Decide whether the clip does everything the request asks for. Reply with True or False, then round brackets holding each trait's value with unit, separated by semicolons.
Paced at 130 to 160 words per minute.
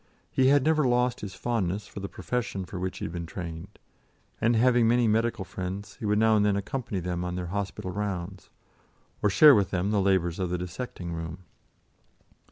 False (195 wpm)